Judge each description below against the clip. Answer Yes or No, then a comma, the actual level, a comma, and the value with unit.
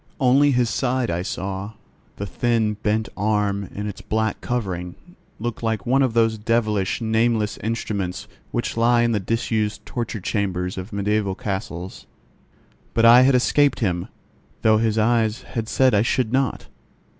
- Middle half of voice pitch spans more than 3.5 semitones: No, average, 2.7 semitones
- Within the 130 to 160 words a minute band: Yes, average, 155 wpm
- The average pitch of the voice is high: No, low, 110 Hz